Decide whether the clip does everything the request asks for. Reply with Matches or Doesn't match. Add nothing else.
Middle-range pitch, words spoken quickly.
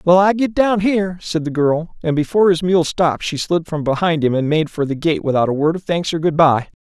Matches